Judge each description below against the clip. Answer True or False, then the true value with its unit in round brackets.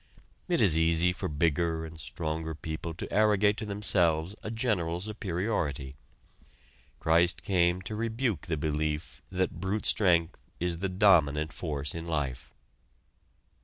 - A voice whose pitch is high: False (85 Hz)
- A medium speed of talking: False (130 wpm)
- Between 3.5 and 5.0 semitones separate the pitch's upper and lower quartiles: True (3.9 semitones)